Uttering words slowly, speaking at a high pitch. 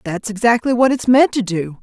No: fast, 230 wpm; high, 220 Hz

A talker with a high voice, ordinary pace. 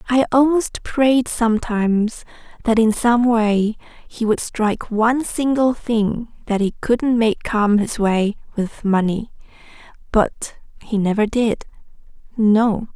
No: high, 225 Hz; slow, 130 wpm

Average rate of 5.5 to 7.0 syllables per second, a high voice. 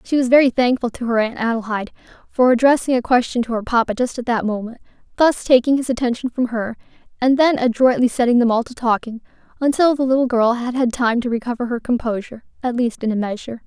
Yes: 6.3 syllables/s; high, 240 Hz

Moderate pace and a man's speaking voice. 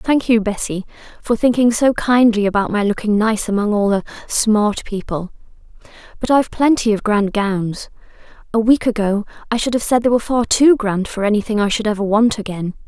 No: average, 185 wpm; female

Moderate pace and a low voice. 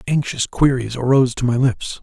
Yes: average, 180 wpm; low, 130 Hz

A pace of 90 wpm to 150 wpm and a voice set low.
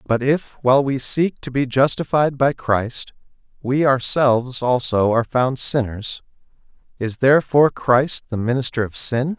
Yes: average, 145 wpm; low, 130 Hz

